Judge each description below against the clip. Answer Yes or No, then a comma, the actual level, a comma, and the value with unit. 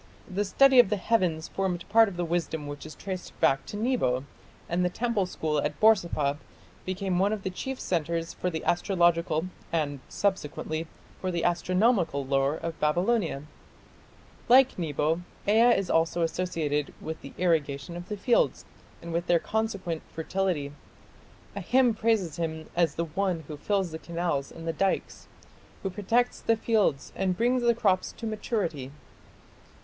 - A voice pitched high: No, medium, 175 Hz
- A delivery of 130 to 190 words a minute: Yes, average, 160 wpm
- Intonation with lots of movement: No, average, 4.2 semitones